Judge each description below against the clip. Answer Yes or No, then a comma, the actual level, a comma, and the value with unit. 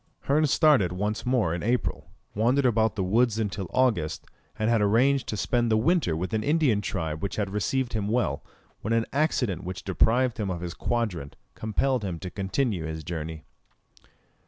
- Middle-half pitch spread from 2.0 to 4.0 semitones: No, average, 5.1 semitones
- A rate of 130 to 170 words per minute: No, average, 180 wpm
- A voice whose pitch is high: No, low, 110 Hz